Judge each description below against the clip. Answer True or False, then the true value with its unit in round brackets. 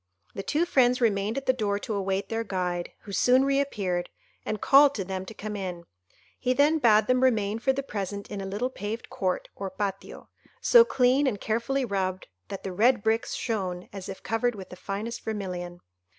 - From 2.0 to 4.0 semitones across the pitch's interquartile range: False (4.5 semitones)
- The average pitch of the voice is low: False (210 Hz)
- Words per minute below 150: False (195 wpm)